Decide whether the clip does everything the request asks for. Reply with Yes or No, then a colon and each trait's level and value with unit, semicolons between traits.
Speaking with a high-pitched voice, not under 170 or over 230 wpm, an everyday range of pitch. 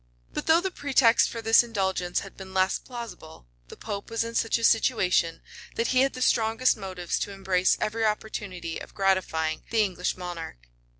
Yes: high, 205 Hz; average, 185 wpm; average, 3.9 semitones